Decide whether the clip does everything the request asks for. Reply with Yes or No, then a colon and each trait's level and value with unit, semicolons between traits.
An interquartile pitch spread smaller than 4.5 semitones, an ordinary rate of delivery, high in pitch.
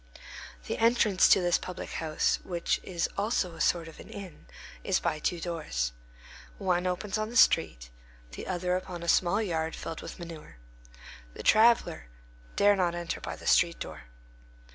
No: average, 2.7 semitones; average, 165 wpm; medium, 175 Hz